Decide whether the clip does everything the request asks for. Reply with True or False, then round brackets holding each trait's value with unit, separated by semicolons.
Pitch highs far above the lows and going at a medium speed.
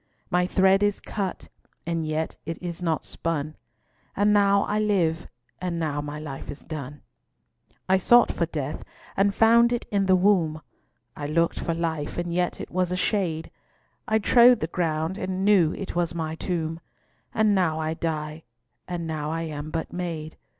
False (3.4 semitones; 175 wpm)